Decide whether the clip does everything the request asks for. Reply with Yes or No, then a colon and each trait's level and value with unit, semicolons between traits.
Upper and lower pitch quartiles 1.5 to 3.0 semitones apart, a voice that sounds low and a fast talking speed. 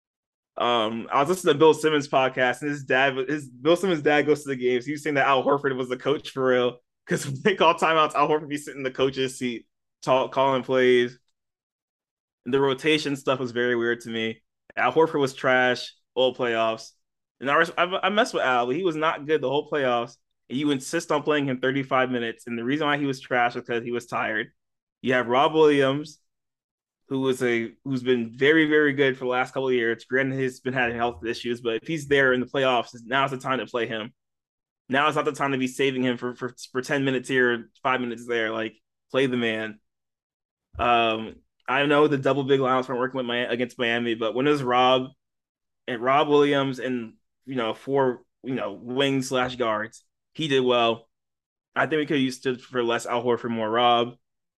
Yes: average, 2.7 semitones; low, 130 Hz; fast, 225 wpm